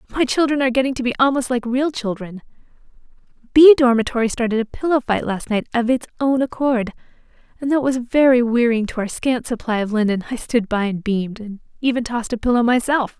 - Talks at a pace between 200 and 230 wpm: Yes, fast, 205 wpm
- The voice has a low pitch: No, high, 240 Hz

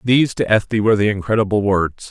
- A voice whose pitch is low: Yes, low, 105 Hz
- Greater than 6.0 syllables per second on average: Yes, 6.5 syllables/s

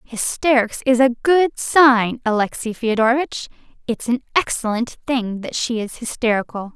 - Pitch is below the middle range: No, high, 240 Hz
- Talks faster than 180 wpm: No, slow, 135 wpm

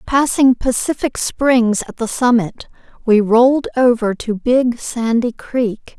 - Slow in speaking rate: Yes, slow, 130 wpm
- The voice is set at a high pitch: Yes, high, 240 Hz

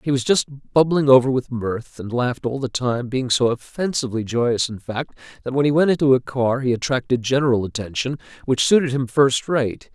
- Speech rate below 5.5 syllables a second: Yes, 5.3 syllables/s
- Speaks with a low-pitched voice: Yes, low, 130 Hz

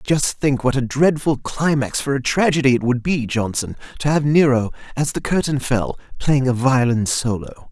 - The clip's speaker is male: Yes, male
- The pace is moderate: Yes, average, 185 wpm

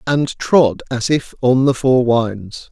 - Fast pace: No, average, 175 wpm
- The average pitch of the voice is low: Yes, low, 125 Hz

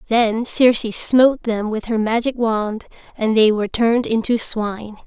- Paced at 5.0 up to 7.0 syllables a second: No, 4.7 syllables/s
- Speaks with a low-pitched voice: No, high, 225 Hz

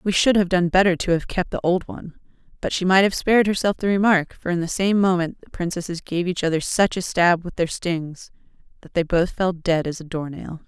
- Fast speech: Yes, fast, 245 wpm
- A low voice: No, medium, 180 Hz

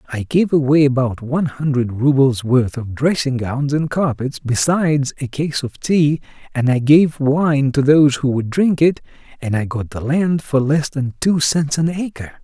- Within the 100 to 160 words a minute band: No, average, 195 wpm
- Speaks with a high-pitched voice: No, medium, 140 Hz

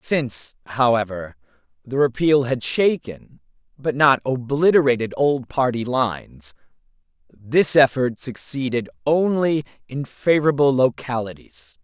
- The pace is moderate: No, slow, 95 wpm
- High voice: No, low, 135 Hz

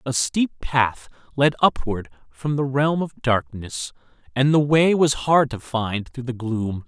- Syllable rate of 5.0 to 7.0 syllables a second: No, 3.9 syllables/s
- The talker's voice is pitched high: No, low, 130 Hz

